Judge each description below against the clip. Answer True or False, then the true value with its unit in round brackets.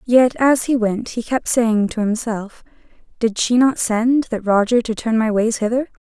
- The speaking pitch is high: True (230 Hz)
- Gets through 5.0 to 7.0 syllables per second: False (4.4 syllables/s)